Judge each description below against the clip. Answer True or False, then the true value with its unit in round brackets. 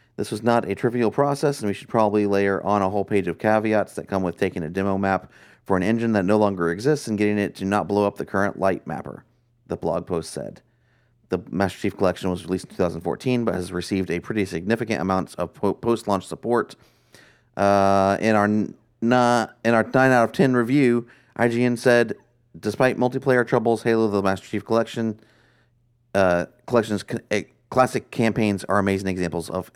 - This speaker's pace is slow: False (195 wpm)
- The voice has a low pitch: True (105 Hz)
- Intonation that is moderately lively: True (3.6 semitones)